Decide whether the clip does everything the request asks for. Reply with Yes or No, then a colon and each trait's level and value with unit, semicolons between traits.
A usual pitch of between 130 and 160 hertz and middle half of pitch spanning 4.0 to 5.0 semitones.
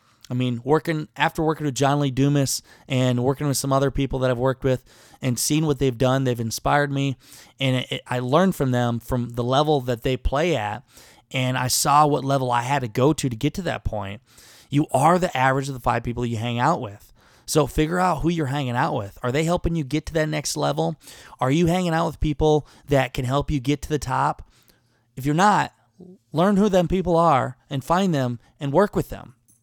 No: medium, 140 Hz; average, 3.6 semitones